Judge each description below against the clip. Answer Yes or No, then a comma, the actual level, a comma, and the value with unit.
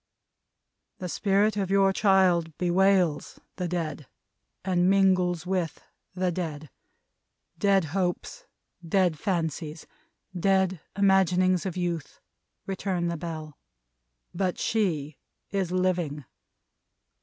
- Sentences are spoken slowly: Yes, slow, 100 wpm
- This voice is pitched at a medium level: Yes, medium, 180 Hz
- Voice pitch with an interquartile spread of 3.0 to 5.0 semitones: No, narrow, 2.5 semitones